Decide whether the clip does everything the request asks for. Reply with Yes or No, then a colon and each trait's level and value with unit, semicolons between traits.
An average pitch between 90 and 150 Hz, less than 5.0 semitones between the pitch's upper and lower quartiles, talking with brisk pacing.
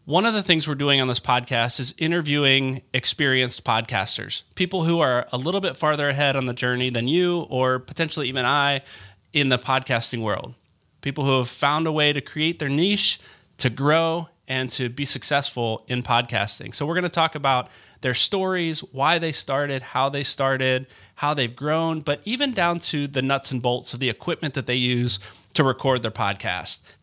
No: low, 135 Hz; average, 3.8 semitones; average, 195 wpm